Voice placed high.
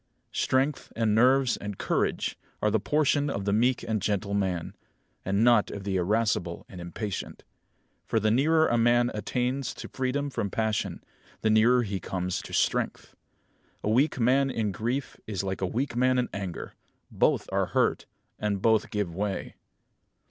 No: low, 110 Hz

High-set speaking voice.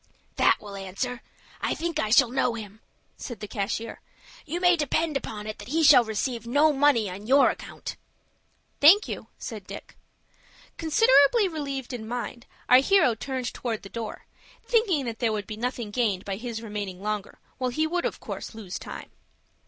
Yes: high, 245 Hz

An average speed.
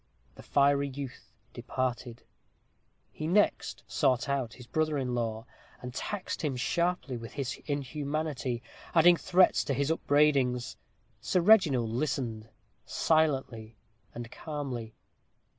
No: slow, 115 wpm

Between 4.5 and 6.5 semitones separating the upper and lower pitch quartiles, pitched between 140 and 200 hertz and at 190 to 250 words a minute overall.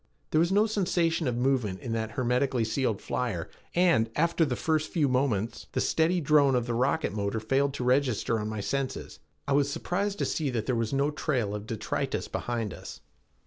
No: average, 5.1 semitones; low, 130 Hz; average, 195 wpm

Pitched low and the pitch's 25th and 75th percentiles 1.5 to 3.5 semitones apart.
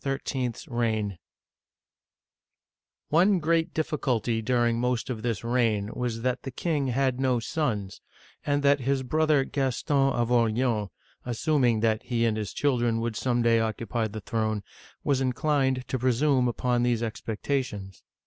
Yes: low, 125 Hz; average, 3.0 semitones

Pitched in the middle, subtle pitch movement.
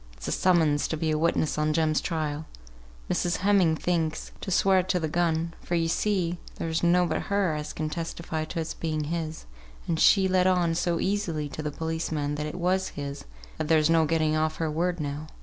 Yes: medium, 165 Hz; narrow, 2.2 semitones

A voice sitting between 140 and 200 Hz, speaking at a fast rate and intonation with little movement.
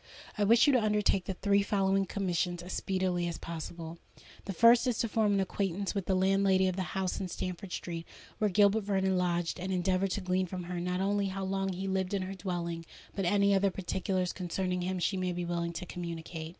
Yes: high, 190 Hz; fast, 215 wpm; narrow, 1.9 semitones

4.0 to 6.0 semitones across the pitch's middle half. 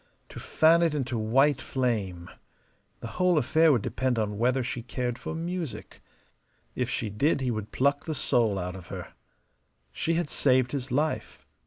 Yes: average, 5.2 semitones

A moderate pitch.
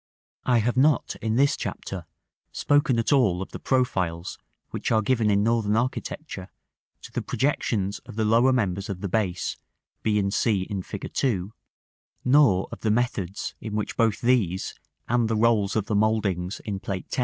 No: low, 110 Hz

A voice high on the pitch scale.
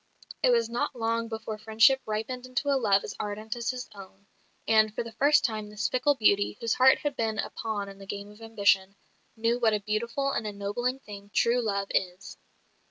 Yes: high, 220 Hz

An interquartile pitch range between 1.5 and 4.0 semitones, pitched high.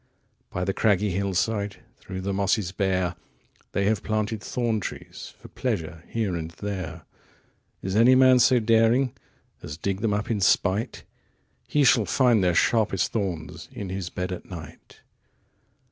No: average, 3.5 semitones; low, 100 Hz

